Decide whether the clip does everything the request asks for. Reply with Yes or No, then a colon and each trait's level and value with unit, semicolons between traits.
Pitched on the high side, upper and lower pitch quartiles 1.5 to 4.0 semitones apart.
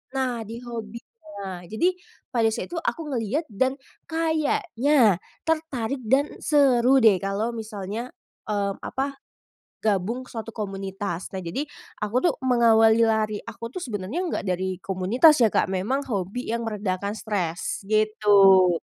No: high, 225 Hz; average, 4.7 semitones